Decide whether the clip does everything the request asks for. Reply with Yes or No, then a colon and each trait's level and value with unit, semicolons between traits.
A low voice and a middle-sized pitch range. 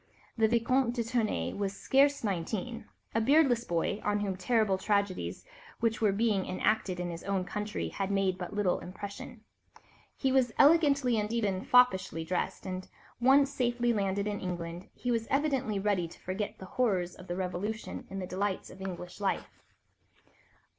No: high, 205 Hz; average, 4.1 semitones